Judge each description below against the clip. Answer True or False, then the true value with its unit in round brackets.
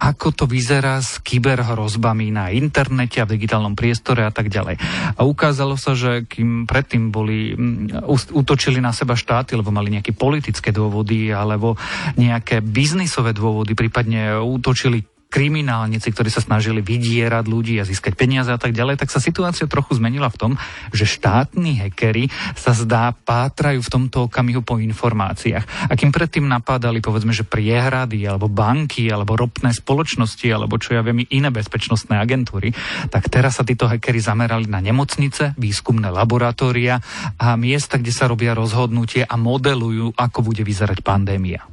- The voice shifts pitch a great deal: False (2.8 semitones)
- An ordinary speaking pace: True (155 wpm)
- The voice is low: True (120 Hz)